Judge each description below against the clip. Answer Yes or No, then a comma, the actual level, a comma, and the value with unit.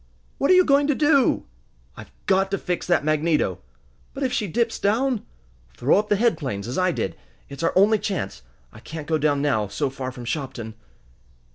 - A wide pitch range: Yes, wide, 8.2 semitones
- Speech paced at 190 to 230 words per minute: Yes, average, 200 wpm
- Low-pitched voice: No, medium, 175 Hz